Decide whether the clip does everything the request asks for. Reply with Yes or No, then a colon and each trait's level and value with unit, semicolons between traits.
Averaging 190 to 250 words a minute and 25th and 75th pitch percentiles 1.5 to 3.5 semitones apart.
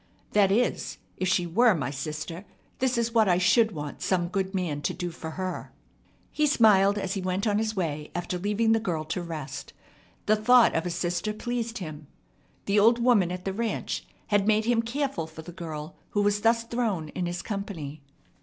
No: average, 200 wpm; average, 4.4 semitones